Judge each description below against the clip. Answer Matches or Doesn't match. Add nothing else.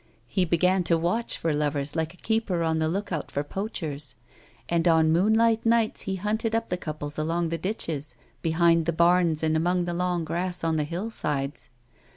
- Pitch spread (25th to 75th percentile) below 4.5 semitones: Matches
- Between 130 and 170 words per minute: Doesn't match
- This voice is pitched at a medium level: Matches